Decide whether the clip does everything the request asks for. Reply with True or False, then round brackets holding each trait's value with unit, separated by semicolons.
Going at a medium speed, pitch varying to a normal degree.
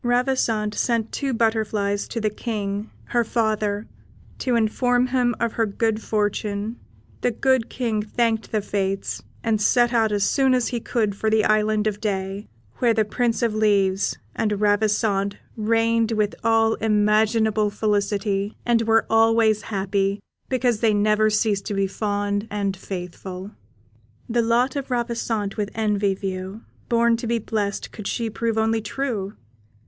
False (155 wpm; 2.1 semitones)